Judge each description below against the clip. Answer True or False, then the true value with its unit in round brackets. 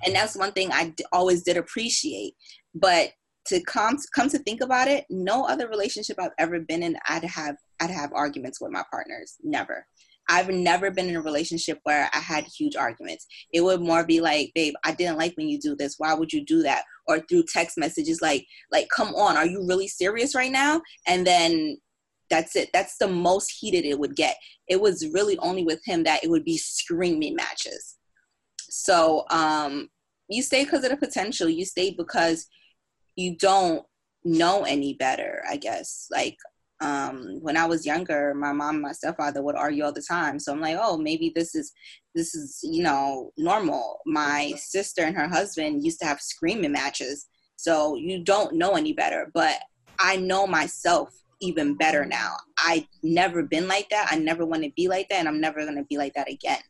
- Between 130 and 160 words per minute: False (200 wpm)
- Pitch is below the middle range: False (180 Hz)